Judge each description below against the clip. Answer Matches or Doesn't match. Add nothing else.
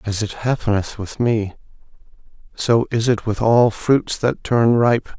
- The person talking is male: Matches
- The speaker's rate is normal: Matches